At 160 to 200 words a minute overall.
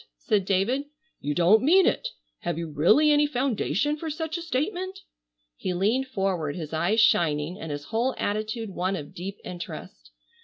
Yes: average, 165 wpm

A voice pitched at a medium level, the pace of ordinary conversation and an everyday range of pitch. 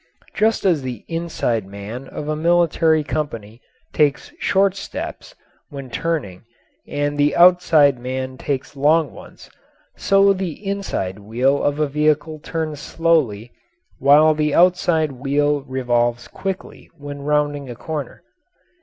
No: medium, 145 Hz; slow, 125 wpm; average, 3.9 semitones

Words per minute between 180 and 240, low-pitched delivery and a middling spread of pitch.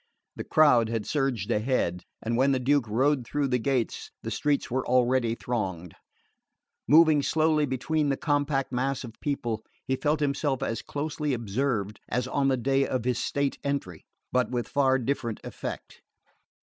No: average, 160 wpm; low, 130 Hz; average, 3.2 semitones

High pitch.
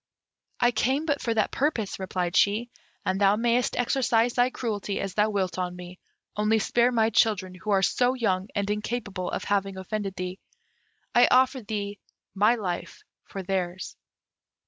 Yes: high, 210 Hz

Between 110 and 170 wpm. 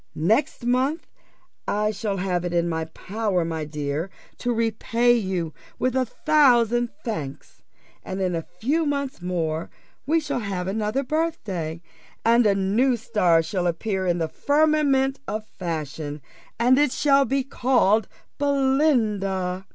Yes: average, 140 wpm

